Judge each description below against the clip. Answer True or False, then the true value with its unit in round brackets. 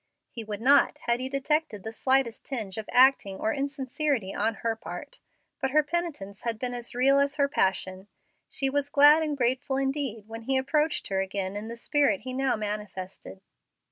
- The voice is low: False (255 Hz)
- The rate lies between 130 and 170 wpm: False (185 wpm)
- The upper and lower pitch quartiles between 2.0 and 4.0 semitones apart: False (4.7 semitones)